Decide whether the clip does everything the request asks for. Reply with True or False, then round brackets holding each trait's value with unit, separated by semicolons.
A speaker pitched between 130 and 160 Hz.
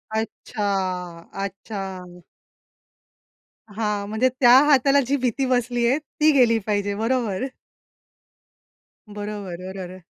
False (220 Hz)